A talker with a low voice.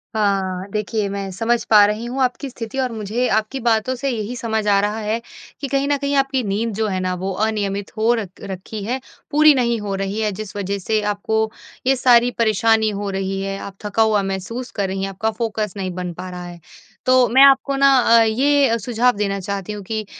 No: high, 215 Hz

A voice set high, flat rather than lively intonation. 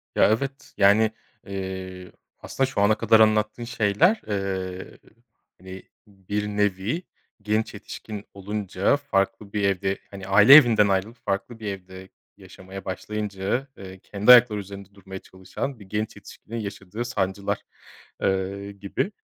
No: low, 100 Hz; narrow, 2.2 semitones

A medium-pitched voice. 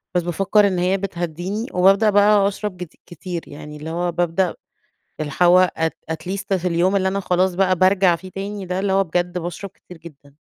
Yes: medium, 180 Hz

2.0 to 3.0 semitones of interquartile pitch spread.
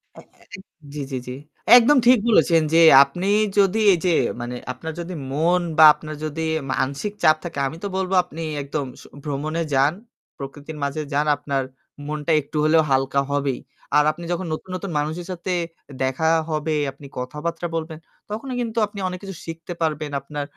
No: average, 3.7 semitones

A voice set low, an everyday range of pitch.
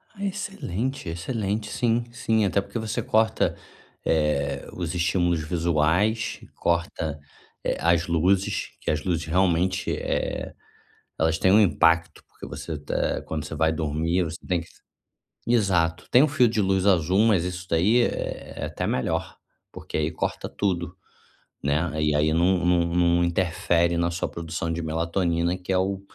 Yes: very low, 85 Hz; average, 3.1 semitones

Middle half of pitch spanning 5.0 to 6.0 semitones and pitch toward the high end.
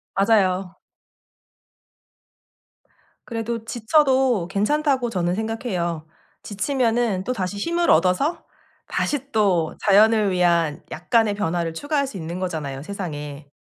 Yes: wide, 5.4 semitones; high, 205 Hz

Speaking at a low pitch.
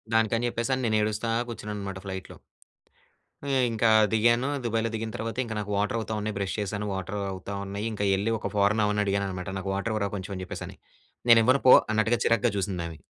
Yes: low, 105 Hz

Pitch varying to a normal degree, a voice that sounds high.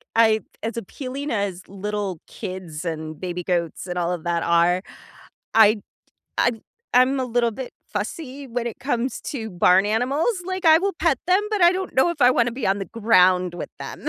No: wide, 6.5 semitones; high, 225 Hz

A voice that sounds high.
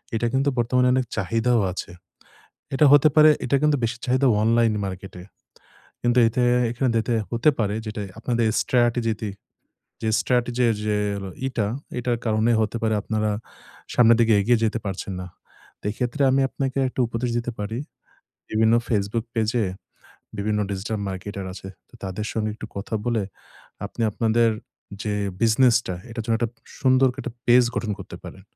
No: low, 115 Hz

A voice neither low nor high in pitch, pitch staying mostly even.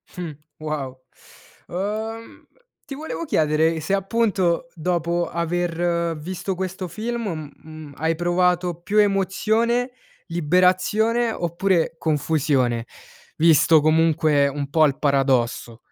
No: medium, 170 Hz; average, 3.8 semitones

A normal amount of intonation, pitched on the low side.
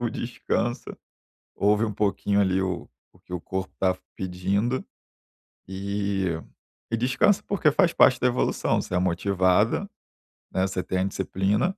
Yes: average, 4.1 semitones; low, 100 Hz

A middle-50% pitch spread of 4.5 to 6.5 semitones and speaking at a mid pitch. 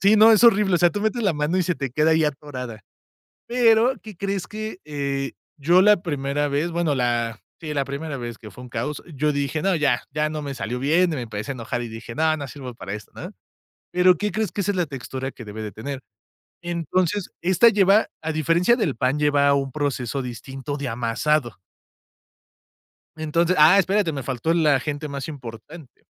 Yes: average, 5.1 semitones; medium, 150 Hz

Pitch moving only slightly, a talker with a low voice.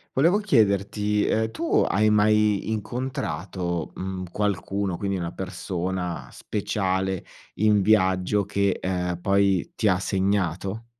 Yes: narrow, 2.3 semitones; low, 100 Hz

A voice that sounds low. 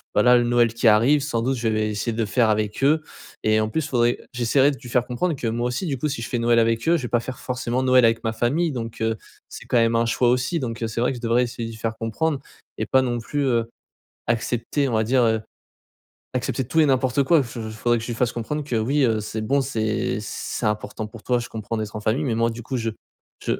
Yes: low, 120 Hz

